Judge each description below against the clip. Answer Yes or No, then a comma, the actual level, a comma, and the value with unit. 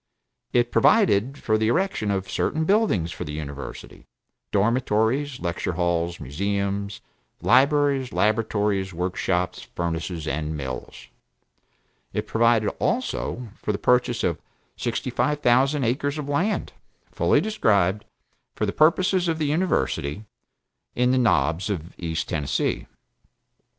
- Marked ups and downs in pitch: Yes, wide, 8.0 semitones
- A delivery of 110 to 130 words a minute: Yes, slow, 125 wpm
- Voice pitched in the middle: No, low, 110 Hz